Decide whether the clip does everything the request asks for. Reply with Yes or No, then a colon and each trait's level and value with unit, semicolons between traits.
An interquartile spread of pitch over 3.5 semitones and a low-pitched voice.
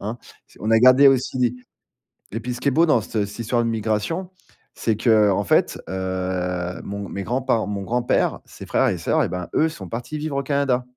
Yes: average, 4.1 semitones; low, 115 Hz